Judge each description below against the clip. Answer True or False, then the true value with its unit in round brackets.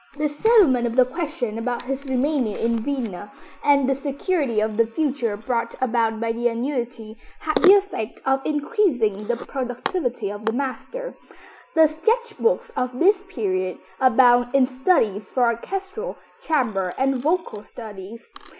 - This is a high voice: True (255 Hz)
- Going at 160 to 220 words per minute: False (150 wpm)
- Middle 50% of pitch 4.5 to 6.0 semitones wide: True (4.9 semitones)